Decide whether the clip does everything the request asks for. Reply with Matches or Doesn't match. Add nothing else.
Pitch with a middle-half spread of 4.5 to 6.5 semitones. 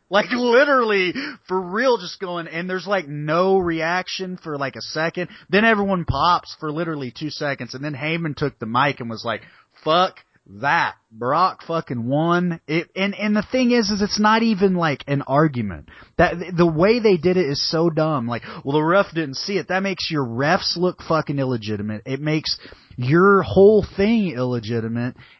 Matches